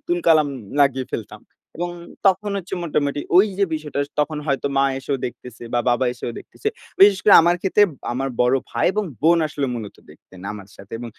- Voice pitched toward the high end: No, medium, 145 Hz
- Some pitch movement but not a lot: No, wide, 5.8 semitones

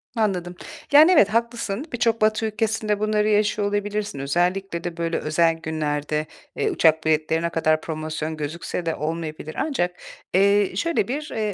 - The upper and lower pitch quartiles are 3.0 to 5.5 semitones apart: Yes, average, 5.2 semitones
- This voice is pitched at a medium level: Yes, medium, 180 Hz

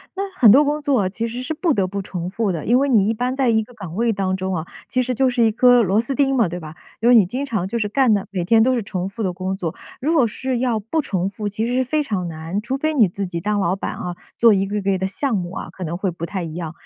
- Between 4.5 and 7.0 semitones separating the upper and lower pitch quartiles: Yes, average, 4.9 semitones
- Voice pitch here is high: Yes, high, 210 Hz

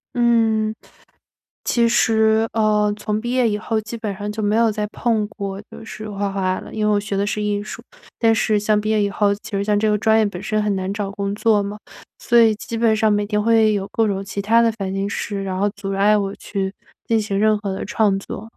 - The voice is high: Yes, high, 210 Hz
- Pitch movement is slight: Yes, narrow, 1.6 semitones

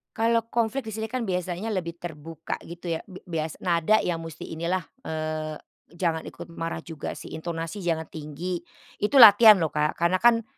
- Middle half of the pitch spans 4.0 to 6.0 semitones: Yes, average, 4.5 semitones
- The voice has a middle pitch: Yes, medium, 170 Hz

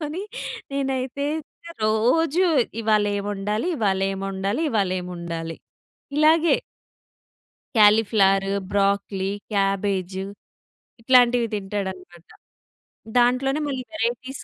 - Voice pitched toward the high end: Yes, high, 215 Hz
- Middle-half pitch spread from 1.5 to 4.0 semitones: No, average, 4.8 semitones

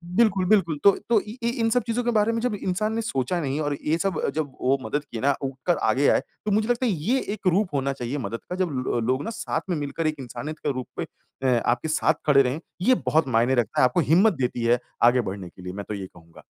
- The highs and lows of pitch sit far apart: Yes, wide, 8.0 semitones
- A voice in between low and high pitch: Yes, medium, 150 Hz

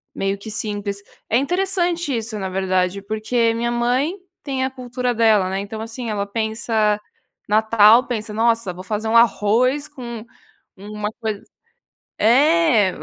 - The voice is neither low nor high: No, high, 225 Hz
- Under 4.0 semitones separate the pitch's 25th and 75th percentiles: Yes, average, 2.9 semitones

